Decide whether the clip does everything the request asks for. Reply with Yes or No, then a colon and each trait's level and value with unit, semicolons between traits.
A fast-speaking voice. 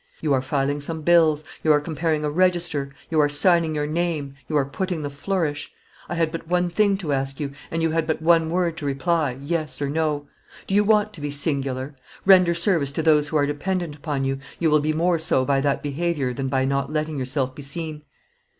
Yes: fast, 225 wpm